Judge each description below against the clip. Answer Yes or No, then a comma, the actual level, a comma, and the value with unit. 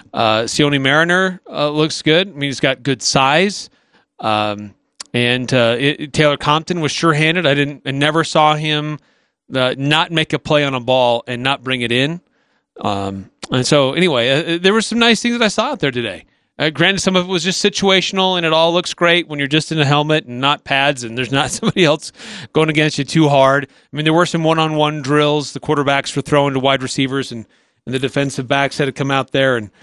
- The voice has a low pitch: No, medium, 145 Hz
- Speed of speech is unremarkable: No, fast, 225 wpm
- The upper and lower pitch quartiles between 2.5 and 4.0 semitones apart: Yes, average, 3.2 semitones